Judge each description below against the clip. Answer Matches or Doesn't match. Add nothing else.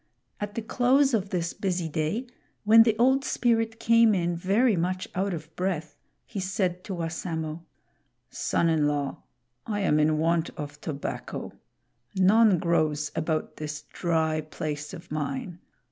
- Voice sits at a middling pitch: Matches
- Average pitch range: Matches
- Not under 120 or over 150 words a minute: Matches